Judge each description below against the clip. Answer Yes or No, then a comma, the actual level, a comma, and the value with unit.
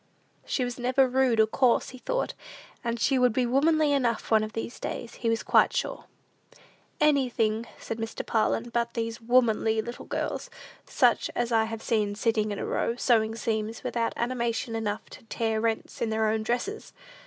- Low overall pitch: No, high, 230 Hz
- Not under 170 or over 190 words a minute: Yes, average, 180 wpm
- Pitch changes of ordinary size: No, narrow, 2.0 semitones